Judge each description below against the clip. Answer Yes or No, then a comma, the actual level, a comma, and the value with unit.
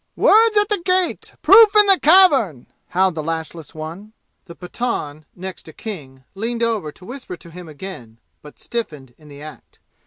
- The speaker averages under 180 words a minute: Yes, average, 165 wpm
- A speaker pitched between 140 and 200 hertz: Yes, medium, 185 Hz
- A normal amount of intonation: No, wide, 8.7 semitones